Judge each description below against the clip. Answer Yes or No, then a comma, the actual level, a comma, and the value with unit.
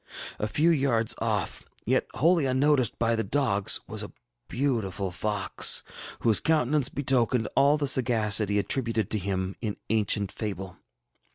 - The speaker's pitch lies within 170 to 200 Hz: No, low, 115 Hz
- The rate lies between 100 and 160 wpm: Yes, average, 140 wpm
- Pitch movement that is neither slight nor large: Yes, average, 4.8 semitones